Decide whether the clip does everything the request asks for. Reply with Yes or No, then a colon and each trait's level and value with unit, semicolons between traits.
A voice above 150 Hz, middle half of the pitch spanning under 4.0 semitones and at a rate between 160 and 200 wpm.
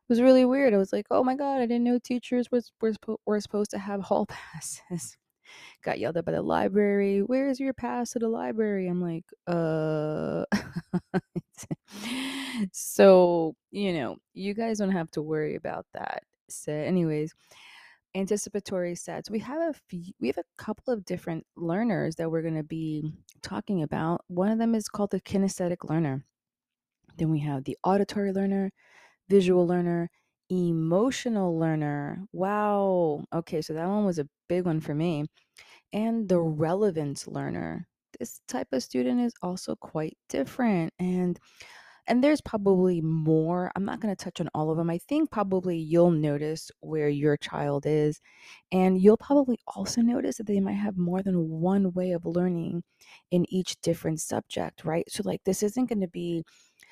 No: medium, 185 Hz; average, 4.3 semitones; average, 170 wpm